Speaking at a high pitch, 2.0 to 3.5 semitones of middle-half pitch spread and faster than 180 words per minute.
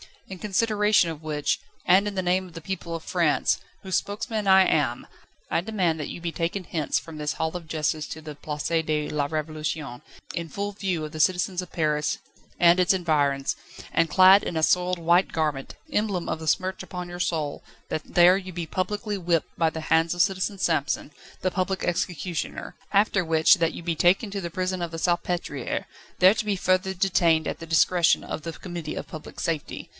No: medium, 175 Hz; average, 2.8 semitones; average, 200 wpm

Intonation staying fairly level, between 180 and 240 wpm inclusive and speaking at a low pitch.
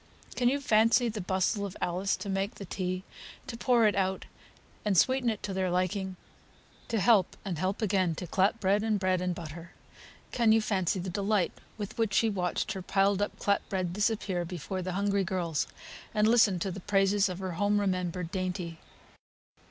No: narrow, 2.3 semitones; average, 190 wpm; high, 195 Hz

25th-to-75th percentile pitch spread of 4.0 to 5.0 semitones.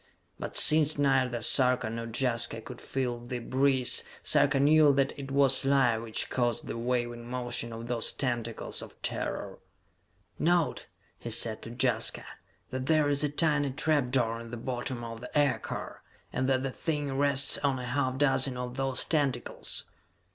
No: average, 2.8 semitones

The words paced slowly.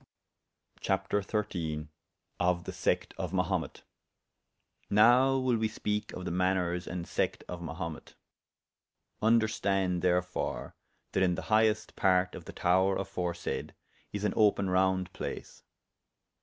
Yes: slow, 120 wpm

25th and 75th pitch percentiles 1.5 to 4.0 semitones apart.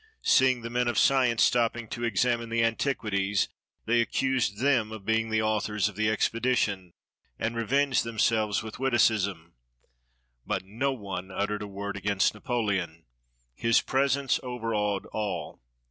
Yes: average, 3.0 semitones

